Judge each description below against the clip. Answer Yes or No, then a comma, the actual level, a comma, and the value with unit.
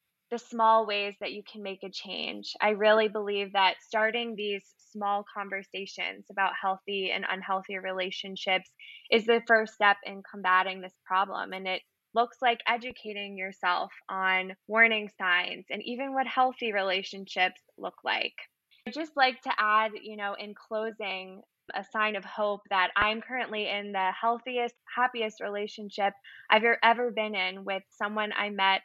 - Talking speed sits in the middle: Yes, average, 160 wpm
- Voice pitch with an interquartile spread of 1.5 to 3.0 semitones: Yes, narrow, 2.6 semitones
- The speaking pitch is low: No, high, 205 Hz